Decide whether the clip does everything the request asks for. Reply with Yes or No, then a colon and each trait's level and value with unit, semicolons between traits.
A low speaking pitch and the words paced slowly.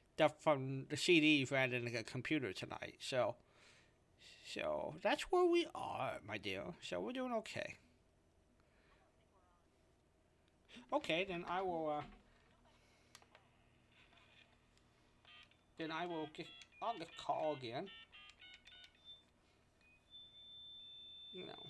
Yes: low, 125 Hz; slow, 95 wpm